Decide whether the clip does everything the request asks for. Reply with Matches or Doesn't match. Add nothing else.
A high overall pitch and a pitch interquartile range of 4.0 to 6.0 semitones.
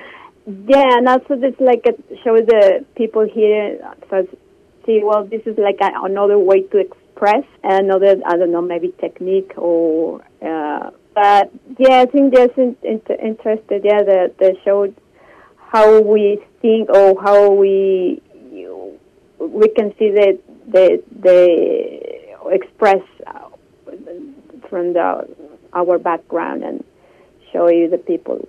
Matches